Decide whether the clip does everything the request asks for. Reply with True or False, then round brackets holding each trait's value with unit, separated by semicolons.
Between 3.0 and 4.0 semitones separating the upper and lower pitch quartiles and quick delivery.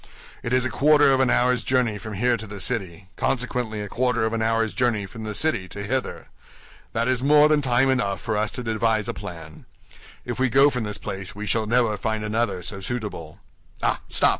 True (3.3 semitones; 215 wpm)